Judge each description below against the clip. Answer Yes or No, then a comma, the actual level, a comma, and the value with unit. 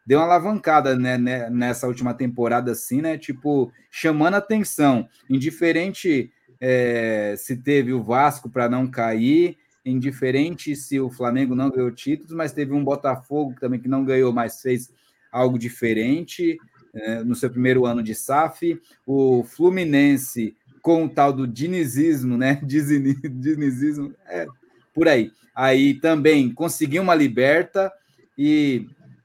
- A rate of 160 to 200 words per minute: No, average, 135 wpm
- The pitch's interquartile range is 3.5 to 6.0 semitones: Yes, average, 3.8 semitones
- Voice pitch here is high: No, low, 135 Hz